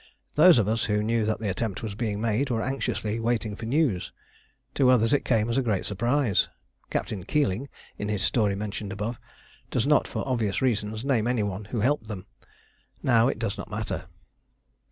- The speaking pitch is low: Yes, low, 110 Hz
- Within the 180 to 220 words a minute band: Yes, average, 190 wpm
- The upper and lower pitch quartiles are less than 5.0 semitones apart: Yes, average, 2.9 semitones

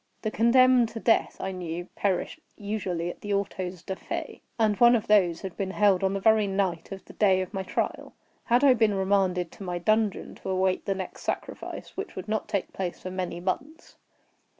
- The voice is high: Yes, high, 195 Hz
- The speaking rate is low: No, fast, 205 wpm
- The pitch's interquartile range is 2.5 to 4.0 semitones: Yes, average, 2.8 semitones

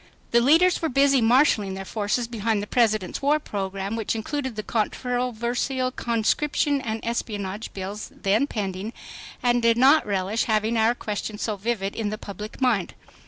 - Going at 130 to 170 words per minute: Yes, average, 160 wpm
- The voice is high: Yes, high, 225 Hz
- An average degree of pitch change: Yes, average, 3.2 semitones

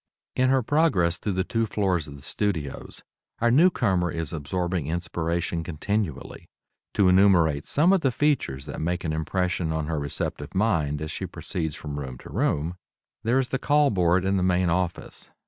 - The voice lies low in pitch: Yes, very low, 90 Hz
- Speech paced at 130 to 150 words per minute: No, average, 180 wpm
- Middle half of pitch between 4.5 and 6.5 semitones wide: Yes, average, 4.8 semitones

